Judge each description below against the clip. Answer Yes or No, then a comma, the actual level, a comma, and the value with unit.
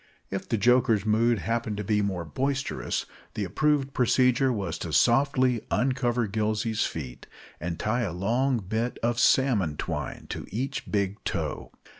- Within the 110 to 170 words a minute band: Yes, average, 150 wpm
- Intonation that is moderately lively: Yes, average, 4.2 semitones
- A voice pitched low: Yes, low, 115 Hz